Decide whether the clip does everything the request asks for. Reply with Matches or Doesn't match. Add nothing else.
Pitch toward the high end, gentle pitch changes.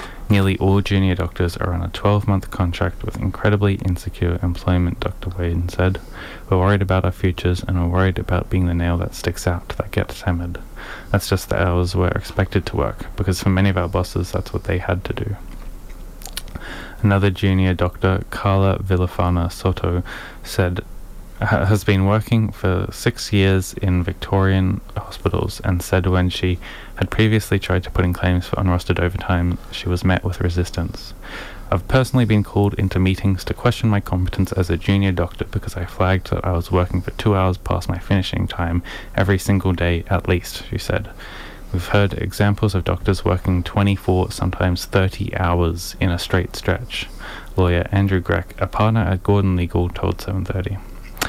Doesn't match